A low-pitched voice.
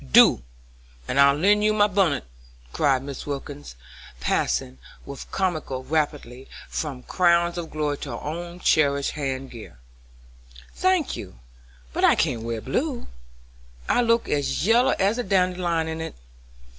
No: medium, 155 Hz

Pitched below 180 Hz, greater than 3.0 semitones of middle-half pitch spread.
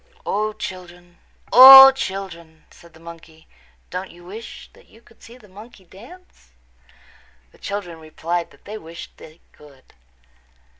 No: medium, 185 Hz; average, 4.4 semitones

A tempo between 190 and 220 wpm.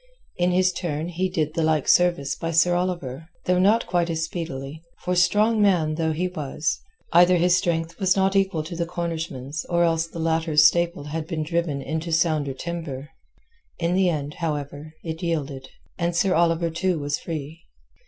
No: average, 180 wpm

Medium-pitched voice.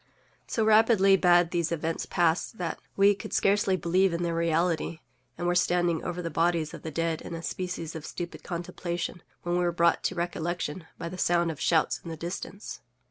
Yes: medium, 175 Hz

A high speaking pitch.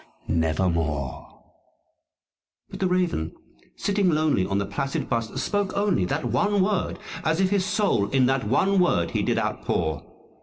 No: low, 135 Hz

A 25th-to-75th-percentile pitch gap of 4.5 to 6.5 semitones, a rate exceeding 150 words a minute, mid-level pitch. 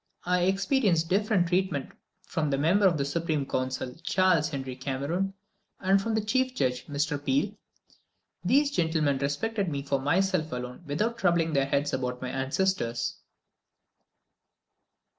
No: wide, 5.6 semitones; average, 140 wpm; medium, 160 Hz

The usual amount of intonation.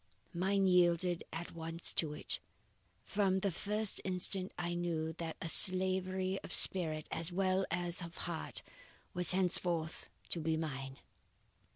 No: narrow, 2.3 semitones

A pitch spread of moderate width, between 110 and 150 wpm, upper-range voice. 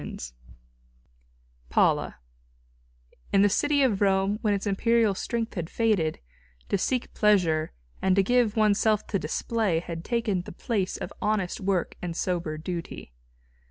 Yes: average, 3.8 semitones; average, 145 wpm; high, 200 Hz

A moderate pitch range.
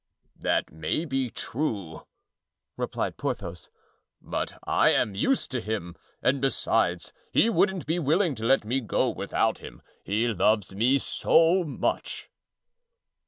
No: wide, 7.1 semitones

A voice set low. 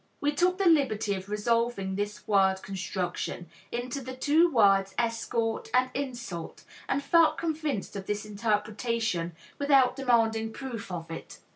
No: high, 230 Hz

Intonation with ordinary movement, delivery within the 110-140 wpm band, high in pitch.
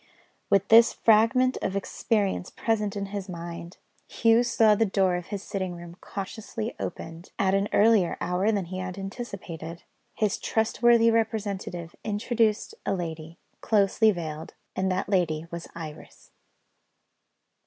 Yes: average, 3.9 semitones; slow, 135 wpm; high, 195 Hz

